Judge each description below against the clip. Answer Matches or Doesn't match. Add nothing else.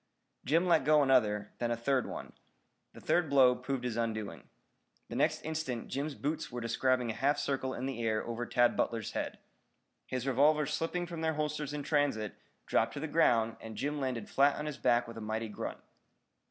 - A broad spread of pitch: Doesn't match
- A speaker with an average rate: Matches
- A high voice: Doesn't match